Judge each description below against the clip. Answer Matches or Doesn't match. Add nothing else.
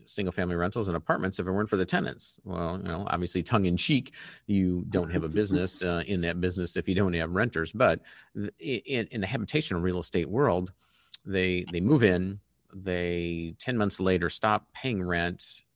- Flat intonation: Matches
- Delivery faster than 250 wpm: Doesn't match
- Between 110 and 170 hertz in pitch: Doesn't match